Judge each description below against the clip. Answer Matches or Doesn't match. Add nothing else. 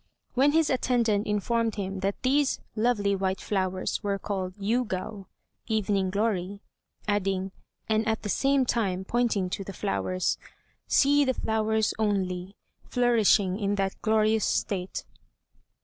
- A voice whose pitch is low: Doesn't match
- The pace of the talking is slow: Matches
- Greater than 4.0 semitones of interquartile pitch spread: Doesn't match